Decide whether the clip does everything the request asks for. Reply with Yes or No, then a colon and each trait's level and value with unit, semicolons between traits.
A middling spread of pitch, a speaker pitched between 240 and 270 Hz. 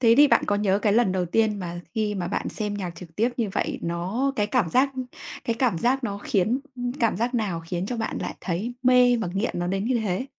No: average, 4.6 semitones; high, 210 Hz